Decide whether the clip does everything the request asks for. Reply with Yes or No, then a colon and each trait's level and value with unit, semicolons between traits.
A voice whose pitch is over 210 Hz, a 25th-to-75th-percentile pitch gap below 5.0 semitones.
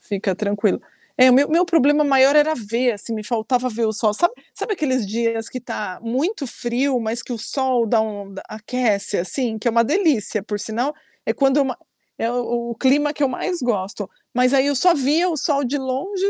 Yes: very high, 250 Hz; average, 4.2 semitones